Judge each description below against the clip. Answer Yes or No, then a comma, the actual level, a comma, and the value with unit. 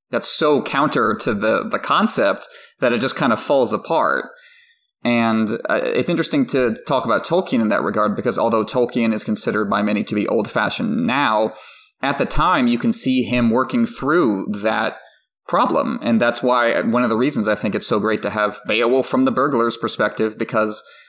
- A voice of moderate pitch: No, low, 120 Hz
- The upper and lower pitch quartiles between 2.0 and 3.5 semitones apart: Yes, average, 2.7 semitones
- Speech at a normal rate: Yes, average, 195 wpm